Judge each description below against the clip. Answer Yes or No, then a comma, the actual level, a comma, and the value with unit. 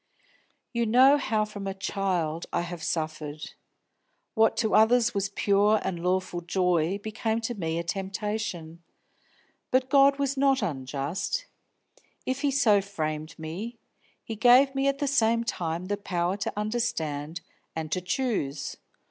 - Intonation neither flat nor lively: No, wide, 5.8 semitones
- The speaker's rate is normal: Yes, average, 145 wpm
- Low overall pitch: No, high, 200 Hz